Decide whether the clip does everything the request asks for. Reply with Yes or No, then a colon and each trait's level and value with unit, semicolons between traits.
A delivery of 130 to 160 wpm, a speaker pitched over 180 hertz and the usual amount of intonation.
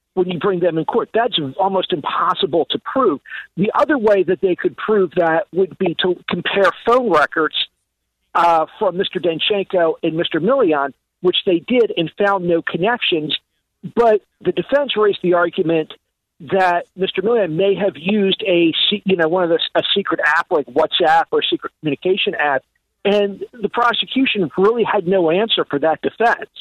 No: average, 175 wpm; high, 190 Hz; average, 3.3 semitones